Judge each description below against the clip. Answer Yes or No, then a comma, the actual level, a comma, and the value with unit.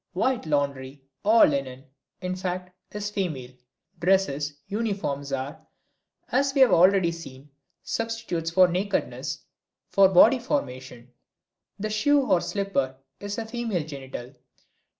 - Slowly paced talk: Yes, slow, 120 wpm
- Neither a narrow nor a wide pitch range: No, wide, 7.1 semitones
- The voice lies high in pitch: No, medium, 180 Hz